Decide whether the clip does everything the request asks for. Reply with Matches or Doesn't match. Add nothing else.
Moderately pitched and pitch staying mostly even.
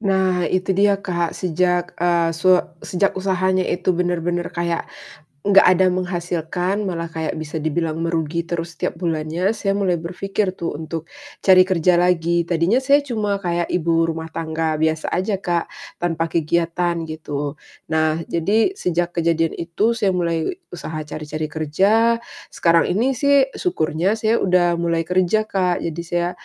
Matches